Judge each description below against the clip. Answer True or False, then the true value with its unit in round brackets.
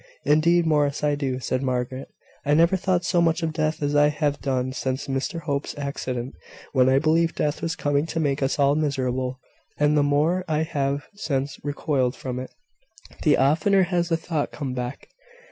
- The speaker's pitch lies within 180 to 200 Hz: False (145 Hz)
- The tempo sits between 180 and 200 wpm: True (185 wpm)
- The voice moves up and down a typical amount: True (3.0 semitones)